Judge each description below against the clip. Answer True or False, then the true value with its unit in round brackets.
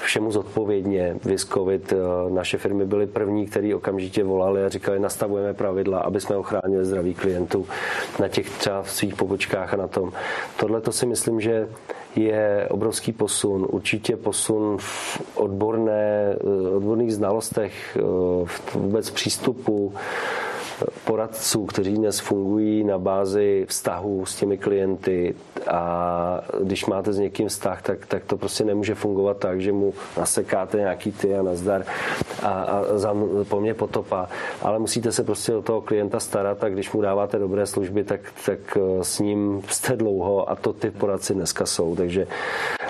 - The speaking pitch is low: True (100 Hz)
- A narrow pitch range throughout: True (1.6 semitones)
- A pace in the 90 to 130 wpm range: False (150 wpm)